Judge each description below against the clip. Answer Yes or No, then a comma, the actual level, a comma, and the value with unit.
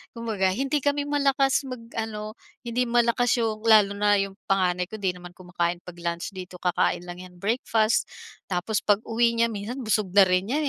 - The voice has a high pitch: Yes, high, 210 Hz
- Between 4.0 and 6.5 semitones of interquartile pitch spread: Yes, average, 4.3 semitones